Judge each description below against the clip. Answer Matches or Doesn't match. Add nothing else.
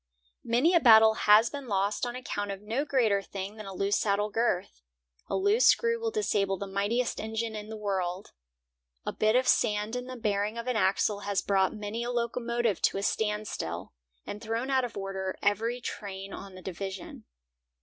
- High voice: Matches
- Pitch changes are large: Doesn't match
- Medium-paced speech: Matches